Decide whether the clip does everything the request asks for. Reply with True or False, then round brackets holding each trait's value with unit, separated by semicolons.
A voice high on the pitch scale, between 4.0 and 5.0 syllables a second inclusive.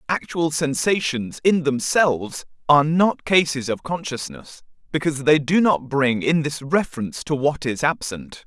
False (150 Hz; 4.7 syllables/s)